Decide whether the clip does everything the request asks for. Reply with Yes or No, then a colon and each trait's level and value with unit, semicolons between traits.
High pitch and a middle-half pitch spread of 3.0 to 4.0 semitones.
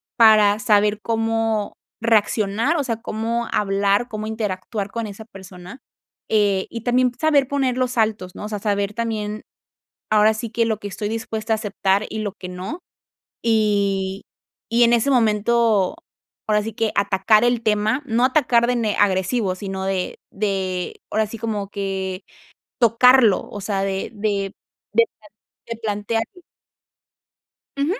No: high, 215 Hz; narrow, 2.4 semitones